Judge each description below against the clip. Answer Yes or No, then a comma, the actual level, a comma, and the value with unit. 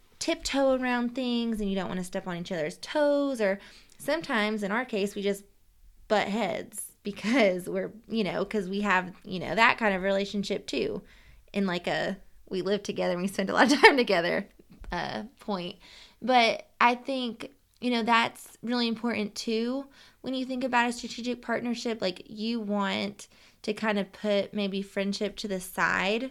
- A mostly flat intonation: No, average, 3.5 semitones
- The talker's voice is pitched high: Yes, high, 210 Hz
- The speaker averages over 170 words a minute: Yes, average, 180 wpm